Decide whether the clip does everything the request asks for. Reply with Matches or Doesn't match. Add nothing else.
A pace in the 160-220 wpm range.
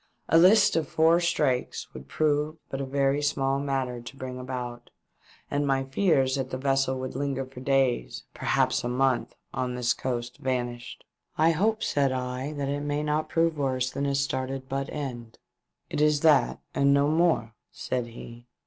Matches